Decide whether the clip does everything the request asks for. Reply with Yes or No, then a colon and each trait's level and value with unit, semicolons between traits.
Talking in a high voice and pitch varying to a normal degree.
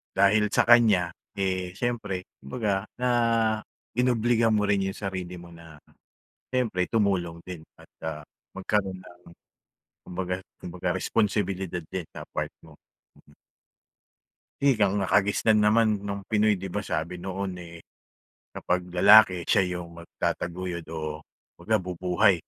No: very low, 95 Hz; average, 3.1 semitones